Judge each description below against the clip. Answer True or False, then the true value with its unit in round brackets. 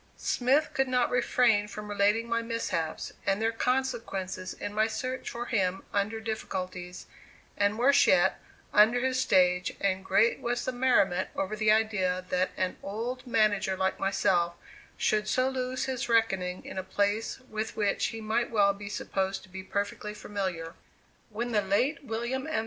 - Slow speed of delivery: False (165 wpm)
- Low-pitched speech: False (215 Hz)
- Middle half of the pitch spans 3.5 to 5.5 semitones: True (3.9 semitones)